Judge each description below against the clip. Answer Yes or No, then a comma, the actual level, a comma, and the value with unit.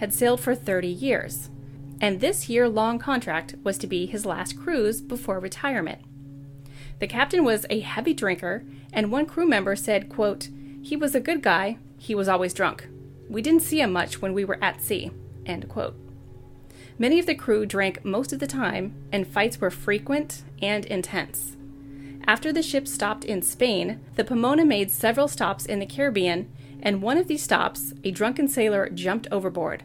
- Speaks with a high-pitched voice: Yes, high, 195 Hz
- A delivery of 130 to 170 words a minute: No, average, 180 wpm